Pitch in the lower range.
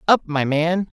No: medium, 165 Hz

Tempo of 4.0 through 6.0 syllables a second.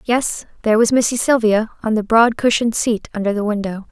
Yes: 5.8 syllables/s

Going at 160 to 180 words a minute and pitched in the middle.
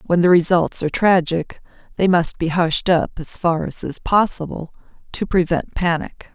Yes: average, 170 wpm; medium, 170 Hz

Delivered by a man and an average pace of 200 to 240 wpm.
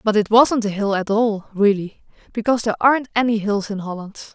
No: female; fast, 205 wpm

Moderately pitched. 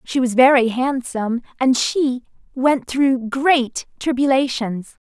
No: very high, 255 Hz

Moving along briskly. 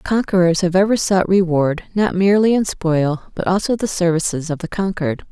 No: average, 180 wpm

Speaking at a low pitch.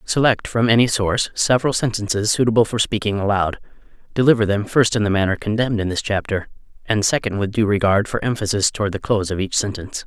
Yes: low, 105 Hz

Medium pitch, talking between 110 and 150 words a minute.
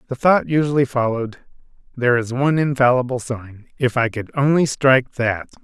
No: low, 130 Hz; average, 140 wpm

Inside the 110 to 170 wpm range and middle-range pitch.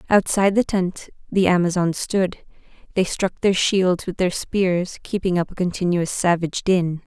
Yes: average, 160 wpm; medium, 180 Hz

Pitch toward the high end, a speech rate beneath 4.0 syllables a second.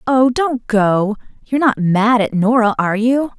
No: high, 230 Hz; 4.5 syllables/s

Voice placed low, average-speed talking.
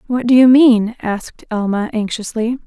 No: high, 230 Hz; average, 155 wpm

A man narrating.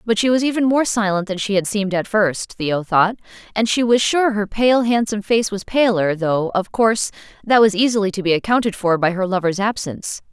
No: female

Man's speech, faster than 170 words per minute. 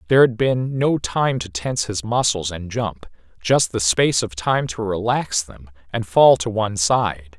Yes: male; average, 195 wpm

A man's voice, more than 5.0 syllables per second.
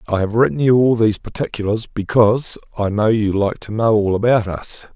Yes: male; 5.5 syllables/s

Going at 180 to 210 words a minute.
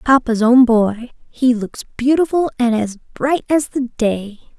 No: average, 155 wpm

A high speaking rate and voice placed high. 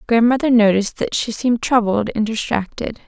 No: average, 155 wpm; high, 225 Hz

